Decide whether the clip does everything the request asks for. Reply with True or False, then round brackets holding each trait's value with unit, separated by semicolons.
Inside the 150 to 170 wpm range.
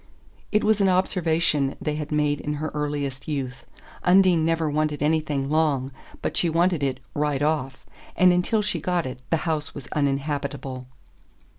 True (160 wpm)